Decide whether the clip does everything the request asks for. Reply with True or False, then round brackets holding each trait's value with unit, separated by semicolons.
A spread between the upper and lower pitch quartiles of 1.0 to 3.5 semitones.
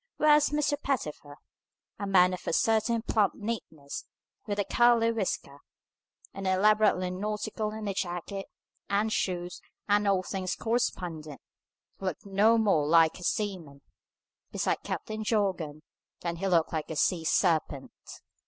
False (4.1 semitones)